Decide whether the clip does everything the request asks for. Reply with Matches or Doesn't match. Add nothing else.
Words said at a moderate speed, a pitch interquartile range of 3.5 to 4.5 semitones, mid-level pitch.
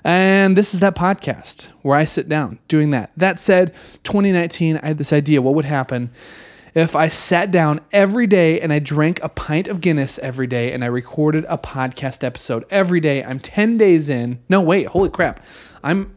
Doesn't match